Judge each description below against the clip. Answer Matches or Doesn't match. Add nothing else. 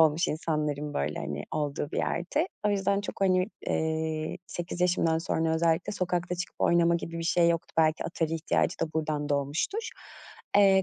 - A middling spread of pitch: Doesn't match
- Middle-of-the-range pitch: Matches